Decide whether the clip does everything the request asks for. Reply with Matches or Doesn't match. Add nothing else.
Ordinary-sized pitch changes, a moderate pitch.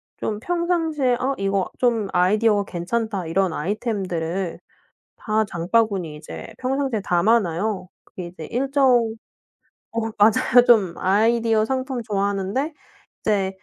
Doesn't match